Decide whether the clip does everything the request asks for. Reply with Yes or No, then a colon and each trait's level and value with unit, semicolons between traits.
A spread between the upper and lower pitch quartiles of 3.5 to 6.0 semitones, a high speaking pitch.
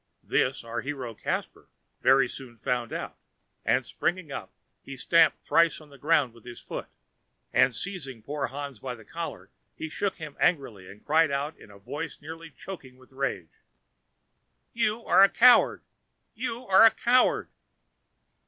No: average, 5.0 semitones; medium, 140 Hz